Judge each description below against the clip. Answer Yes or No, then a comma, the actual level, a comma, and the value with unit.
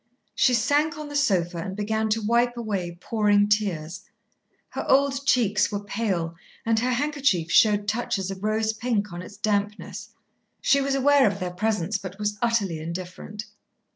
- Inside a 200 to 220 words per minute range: No, average, 165 wpm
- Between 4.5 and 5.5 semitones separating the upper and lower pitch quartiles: No, average, 3.7 semitones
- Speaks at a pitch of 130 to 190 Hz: No, high, 210 Hz